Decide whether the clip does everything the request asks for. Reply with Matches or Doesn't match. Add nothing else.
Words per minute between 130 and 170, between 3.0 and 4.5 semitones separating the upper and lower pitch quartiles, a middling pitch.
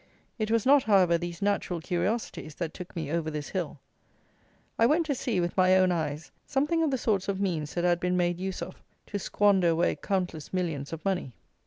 Doesn't match